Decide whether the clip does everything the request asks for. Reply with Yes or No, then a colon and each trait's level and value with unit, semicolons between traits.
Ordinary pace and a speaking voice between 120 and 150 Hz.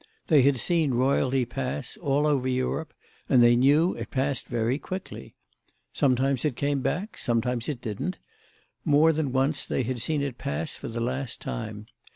Yes: average, 170 wpm; low, 135 Hz